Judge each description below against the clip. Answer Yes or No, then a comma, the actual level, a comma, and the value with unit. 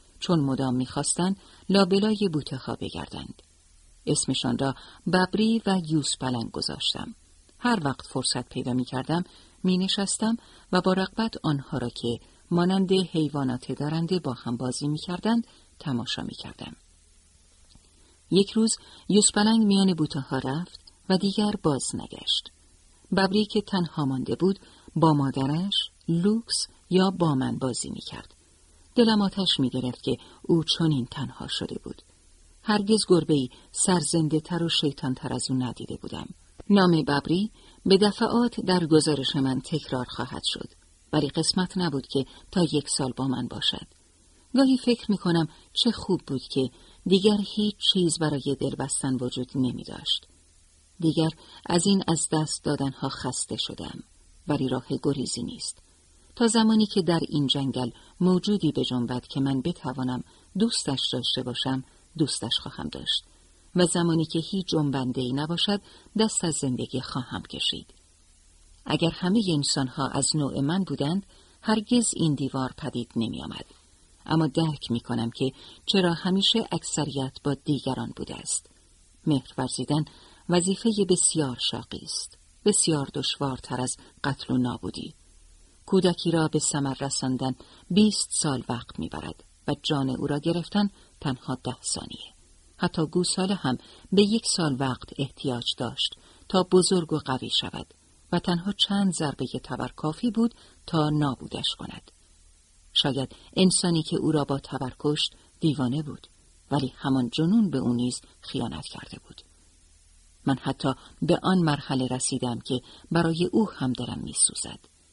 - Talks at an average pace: Yes, average, 140 wpm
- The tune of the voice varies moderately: No, wide, 6.3 semitones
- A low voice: No, medium, 145 Hz